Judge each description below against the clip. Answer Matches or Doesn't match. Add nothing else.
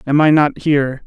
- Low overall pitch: Doesn't match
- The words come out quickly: Matches